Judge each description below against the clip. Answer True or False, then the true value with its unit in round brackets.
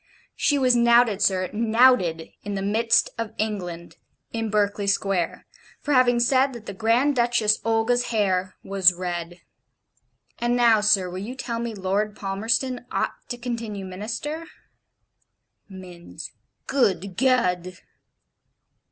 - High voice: True (215 Hz)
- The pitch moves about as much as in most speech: True (4.0 semitones)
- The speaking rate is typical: False (125 wpm)